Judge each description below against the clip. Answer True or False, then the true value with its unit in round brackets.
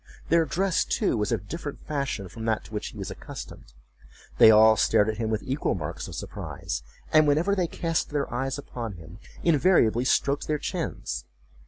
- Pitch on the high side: False (130 Hz)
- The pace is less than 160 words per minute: False (190 wpm)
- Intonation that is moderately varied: False (6.0 semitones)